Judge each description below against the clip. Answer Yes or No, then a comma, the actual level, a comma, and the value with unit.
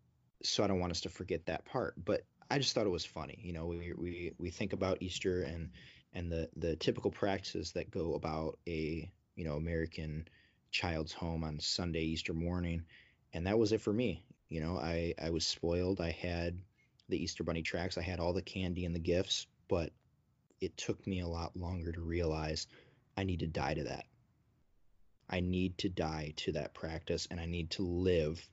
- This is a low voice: Yes, very low, 85 Hz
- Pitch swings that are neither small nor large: No, narrow, 2.0 semitones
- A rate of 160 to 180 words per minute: No, average, 200 wpm